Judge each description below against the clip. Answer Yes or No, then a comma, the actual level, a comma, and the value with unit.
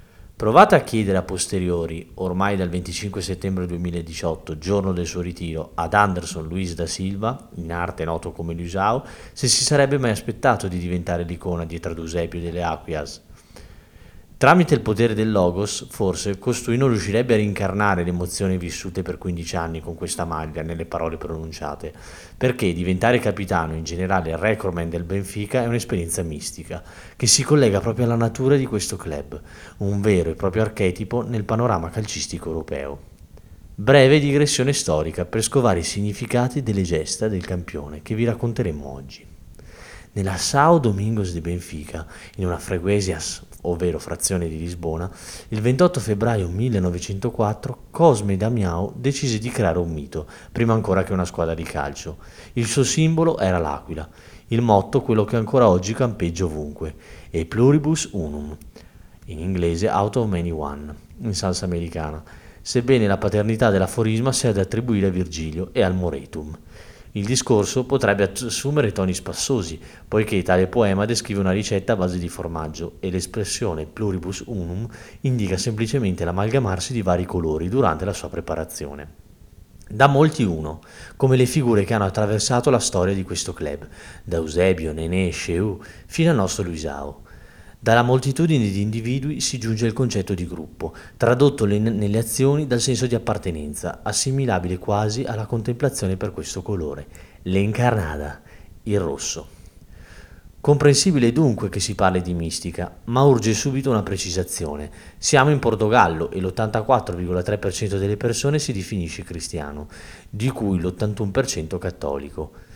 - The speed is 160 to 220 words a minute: No, average, 145 wpm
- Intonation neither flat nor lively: Yes, average, 4.9 semitones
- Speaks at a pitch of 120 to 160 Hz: No, very low, 95 Hz